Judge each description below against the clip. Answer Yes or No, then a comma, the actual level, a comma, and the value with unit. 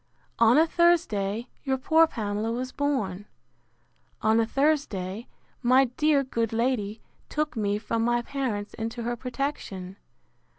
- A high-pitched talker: Yes, high, 240 Hz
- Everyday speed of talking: No, slow, 130 wpm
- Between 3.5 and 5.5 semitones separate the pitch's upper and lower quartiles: Yes, average, 4.5 semitones